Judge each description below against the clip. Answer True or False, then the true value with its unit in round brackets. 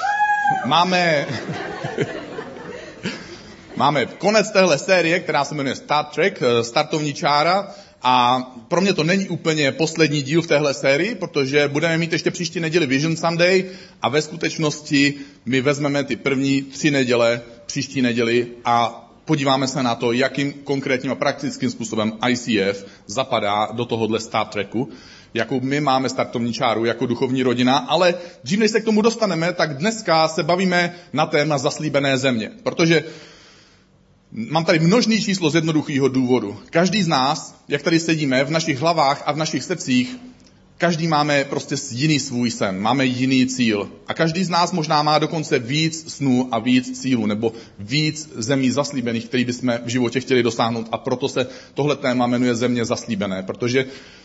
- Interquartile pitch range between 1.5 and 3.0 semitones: False (4.8 semitones)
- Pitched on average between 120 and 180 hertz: True (140 Hz)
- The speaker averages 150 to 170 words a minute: True (155 wpm)